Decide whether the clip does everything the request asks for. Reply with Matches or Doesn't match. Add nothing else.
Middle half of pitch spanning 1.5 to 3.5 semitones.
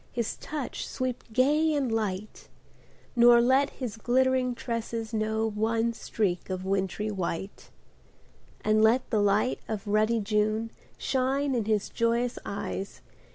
Matches